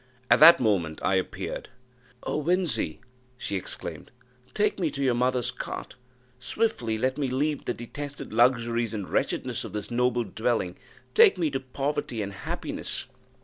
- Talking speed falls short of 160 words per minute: Yes, average, 150 wpm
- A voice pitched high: No, low, 125 Hz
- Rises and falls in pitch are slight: No, average, 4.7 semitones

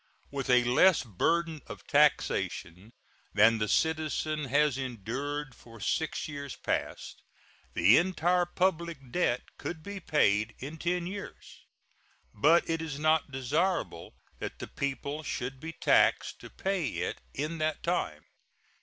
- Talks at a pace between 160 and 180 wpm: No, slow, 135 wpm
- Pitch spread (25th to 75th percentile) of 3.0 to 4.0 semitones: No, average, 4.8 semitones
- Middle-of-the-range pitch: Yes, medium, 150 Hz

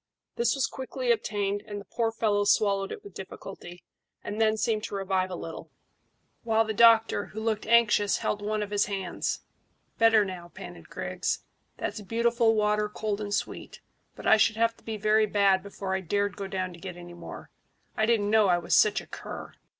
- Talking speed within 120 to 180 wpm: No, average, 195 wpm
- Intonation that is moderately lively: No, narrow, 2.1 semitones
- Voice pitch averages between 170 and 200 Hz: No, high, 210 Hz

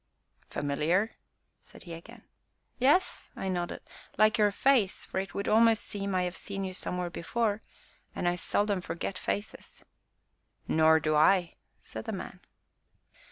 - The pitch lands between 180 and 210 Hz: Yes, high, 190 Hz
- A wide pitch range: No, average, 3.4 semitones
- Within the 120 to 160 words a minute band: Yes, average, 150 wpm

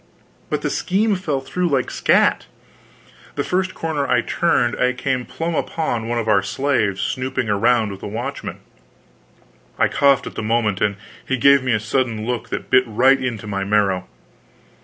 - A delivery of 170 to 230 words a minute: Yes, average, 175 wpm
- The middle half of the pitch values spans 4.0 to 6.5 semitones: Yes, average, 4.4 semitones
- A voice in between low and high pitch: No, low, 125 Hz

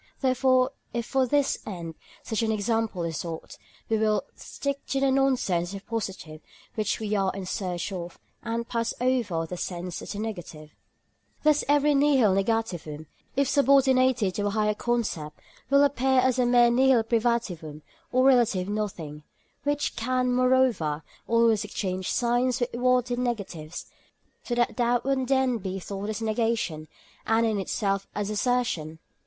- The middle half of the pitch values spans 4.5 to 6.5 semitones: Yes, average, 5.0 semitones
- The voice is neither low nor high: No, high, 225 Hz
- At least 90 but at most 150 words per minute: No, average, 160 wpm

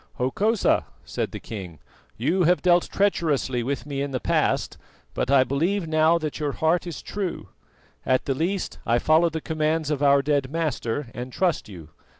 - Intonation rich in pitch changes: No, average, 4.4 semitones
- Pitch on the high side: No, medium, 150 Hz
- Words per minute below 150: No, average, 175 wpm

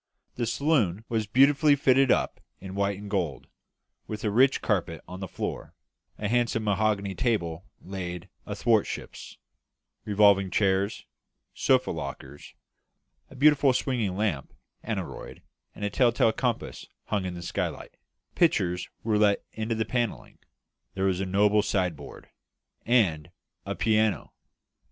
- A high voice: No, low, 105 Hz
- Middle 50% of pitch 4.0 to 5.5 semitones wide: No, average, 3.4 semitones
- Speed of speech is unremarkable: No, slow, 130 wpm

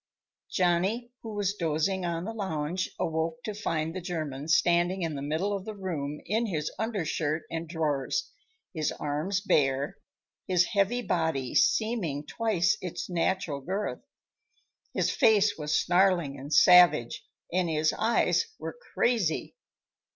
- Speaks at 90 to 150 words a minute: Yes, slow, 135 wpm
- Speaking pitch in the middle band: Yes, medium, 175 Hz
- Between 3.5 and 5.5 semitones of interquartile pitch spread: Yes, average, 4.3 semitones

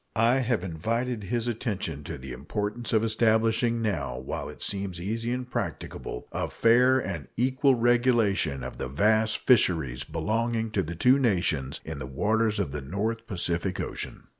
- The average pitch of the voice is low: Yes, low, 110 Hz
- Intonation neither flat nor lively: No, wide, 5.9 semitones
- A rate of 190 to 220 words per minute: No, average, 165 wpm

